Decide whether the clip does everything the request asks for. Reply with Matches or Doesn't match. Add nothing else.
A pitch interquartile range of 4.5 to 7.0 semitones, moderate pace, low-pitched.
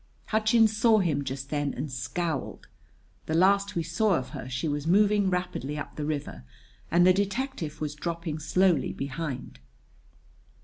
Doesn't match